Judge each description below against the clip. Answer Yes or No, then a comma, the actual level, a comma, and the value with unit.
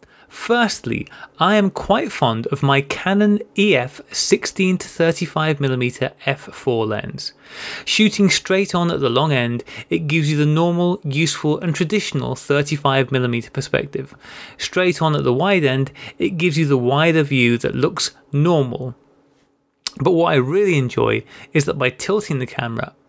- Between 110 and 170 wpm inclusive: Yes, average, 145 wpm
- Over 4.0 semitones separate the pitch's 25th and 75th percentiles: Yes, average, 5.2 semitones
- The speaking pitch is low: No, medium, 150 Hz